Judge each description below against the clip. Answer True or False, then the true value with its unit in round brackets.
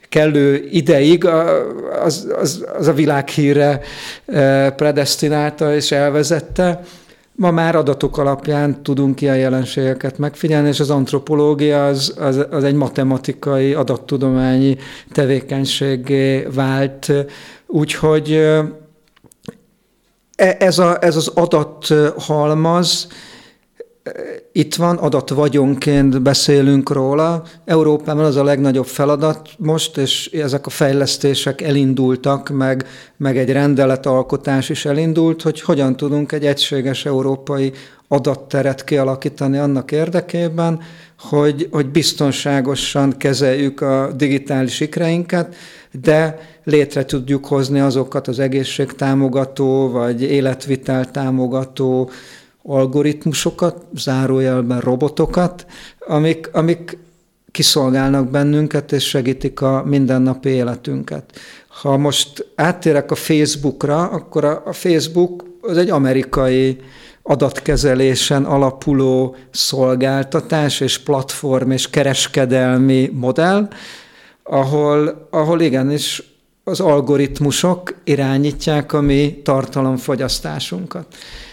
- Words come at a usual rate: False (90 wpm)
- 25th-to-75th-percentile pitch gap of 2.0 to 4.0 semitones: True (2.5 semitones)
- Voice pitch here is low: False (145 Hz)